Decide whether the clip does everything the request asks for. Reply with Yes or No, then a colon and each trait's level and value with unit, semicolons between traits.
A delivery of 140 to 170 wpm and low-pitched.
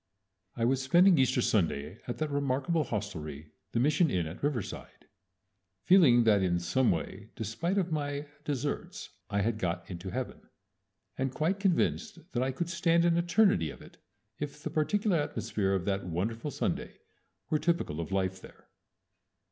Yes: average, 160 wpm; low, 130 Hz